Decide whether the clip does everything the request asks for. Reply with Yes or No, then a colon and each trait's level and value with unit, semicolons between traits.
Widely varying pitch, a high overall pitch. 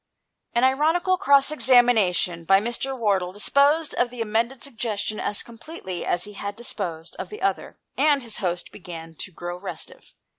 Yes: wide, 6.3 semitones; high, 225 Hz